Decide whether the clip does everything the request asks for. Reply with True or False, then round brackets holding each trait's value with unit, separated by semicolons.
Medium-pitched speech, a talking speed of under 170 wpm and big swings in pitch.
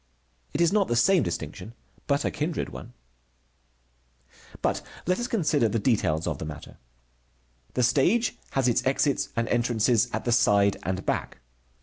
False (120 Hz; 155 wpm; 6.6 semitones)